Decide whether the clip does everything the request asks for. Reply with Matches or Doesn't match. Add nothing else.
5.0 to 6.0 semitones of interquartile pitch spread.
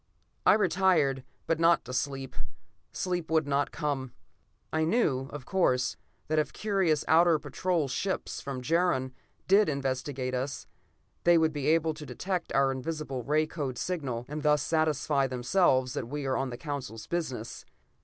Doesn't match